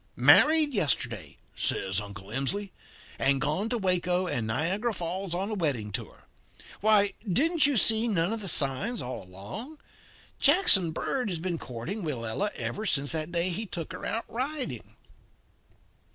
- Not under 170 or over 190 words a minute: No, average, 150 wpm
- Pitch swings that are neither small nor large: No, wide, 8.0 semitones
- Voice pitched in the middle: Yes, medium, 180 Hz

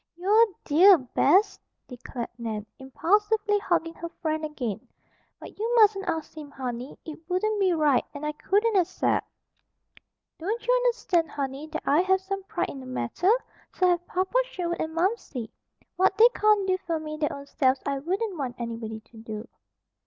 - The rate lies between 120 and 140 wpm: No, average, 175 wpm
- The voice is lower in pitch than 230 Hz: No, very high, 330 Hz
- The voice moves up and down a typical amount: No, wide, 6.3 semitones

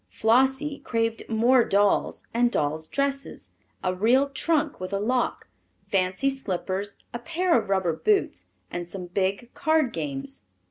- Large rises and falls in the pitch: Yes, wide, 6.5 semitones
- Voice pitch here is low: No, high, 225 Hz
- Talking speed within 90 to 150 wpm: Yes, average, 140 wpm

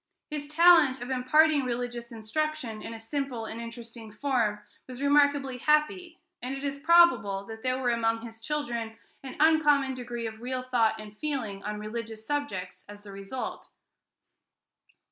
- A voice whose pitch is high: Yes, very high, 250 Hz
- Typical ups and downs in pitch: Yes, average, 4.3 semitones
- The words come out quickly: No, average, 155 wpm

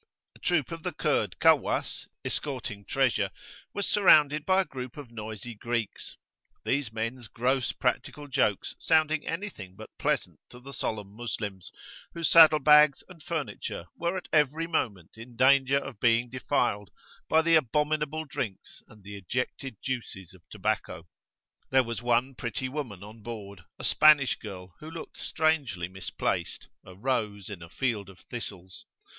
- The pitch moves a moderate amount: No, wide, 6.2 semitones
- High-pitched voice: No, low, 125 Hz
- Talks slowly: No, average, 150 wpm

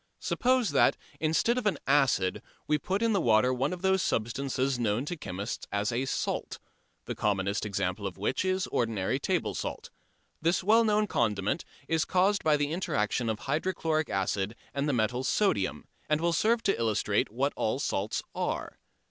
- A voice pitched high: No, low, 135 Hz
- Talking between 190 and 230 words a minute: No, average, 175 wpm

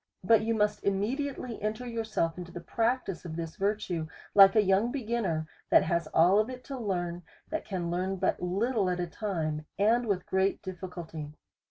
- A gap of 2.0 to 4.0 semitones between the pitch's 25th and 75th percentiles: No, average, 4.4 semitones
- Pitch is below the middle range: No, high, 195 Hz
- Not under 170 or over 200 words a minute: Yes, average, 190 wpm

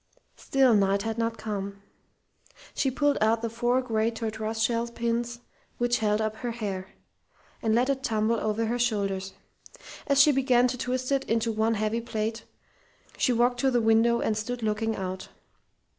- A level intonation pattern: Yes, narrow, 2.0 semitones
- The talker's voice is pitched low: No, high, 230 Hz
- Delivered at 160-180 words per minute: Yes, average, 170 wpm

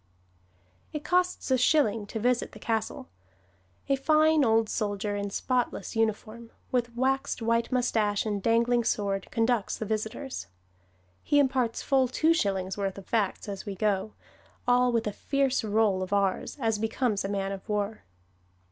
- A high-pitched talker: Yes, high, 225 Hz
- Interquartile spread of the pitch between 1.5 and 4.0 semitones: Yes, average, 3.6 semitones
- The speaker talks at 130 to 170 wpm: Yes, average, 155 wpm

